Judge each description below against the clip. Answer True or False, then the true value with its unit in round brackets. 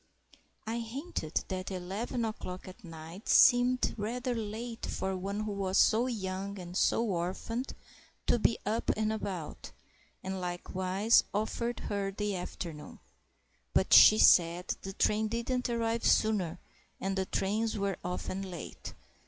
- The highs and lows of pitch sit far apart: False (3.5 semitones)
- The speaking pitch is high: True (200 Hz)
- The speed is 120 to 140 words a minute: True (135 wpm)